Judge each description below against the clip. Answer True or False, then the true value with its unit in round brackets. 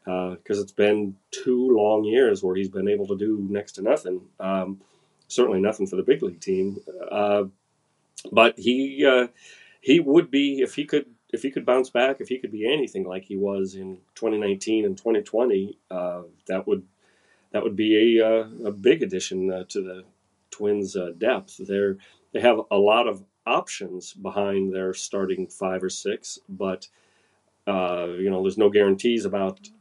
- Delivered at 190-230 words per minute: False (175 wpm)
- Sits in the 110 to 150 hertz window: False (100 Hz)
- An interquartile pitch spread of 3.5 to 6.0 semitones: False (3.0 semitones)